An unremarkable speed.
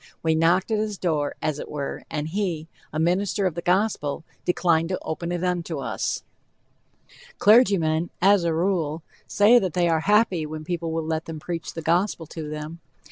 Yes: average, 185 wpm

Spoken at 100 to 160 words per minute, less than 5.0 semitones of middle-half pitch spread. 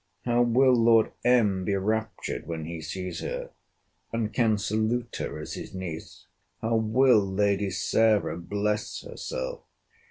Yes: slow, 135 wpm; average, 3.7 semitones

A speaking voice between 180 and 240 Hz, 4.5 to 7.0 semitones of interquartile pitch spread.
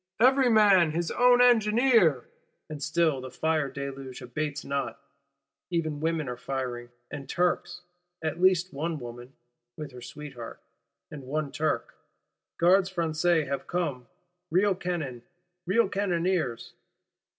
No: medium, 155 Hz; average, 4.8 semitones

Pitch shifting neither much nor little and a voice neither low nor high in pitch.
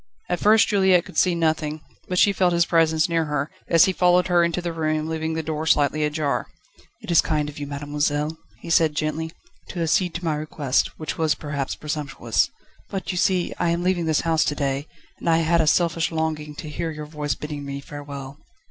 No: narrow, 2.3 semitones; medium, 160 Hz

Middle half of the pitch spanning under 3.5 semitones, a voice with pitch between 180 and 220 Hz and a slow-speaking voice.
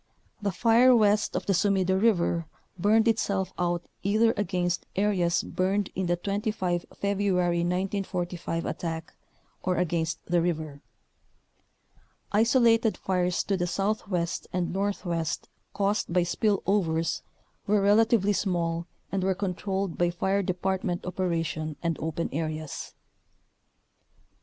Yes: average, 2.8 semitones; medium, 185 Hz; slow, 120 wpm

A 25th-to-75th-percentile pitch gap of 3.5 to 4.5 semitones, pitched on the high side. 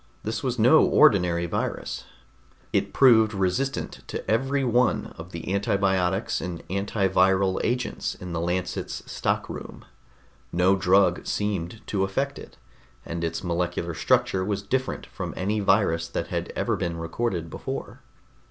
No: average, 4.1 semitones; very low, 95 Hz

